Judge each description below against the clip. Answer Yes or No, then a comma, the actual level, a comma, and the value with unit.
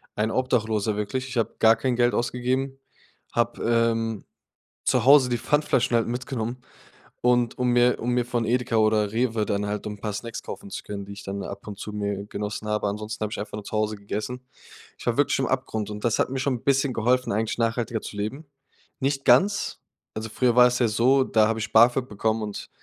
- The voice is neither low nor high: No, low, 115 Hz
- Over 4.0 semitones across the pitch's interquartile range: No, average, 2.8 semitones